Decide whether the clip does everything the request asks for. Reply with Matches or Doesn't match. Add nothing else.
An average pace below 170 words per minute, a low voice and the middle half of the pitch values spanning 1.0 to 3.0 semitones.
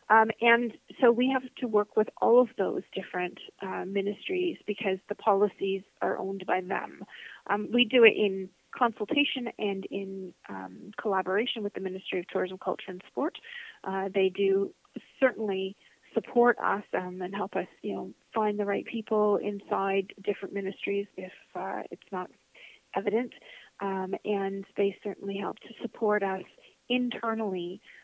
Doesn't match